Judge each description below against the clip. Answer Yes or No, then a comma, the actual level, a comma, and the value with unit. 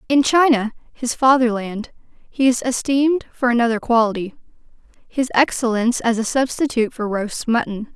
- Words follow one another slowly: Yes, slow, 130 wpm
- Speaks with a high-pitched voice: Yes, high, 240 Hz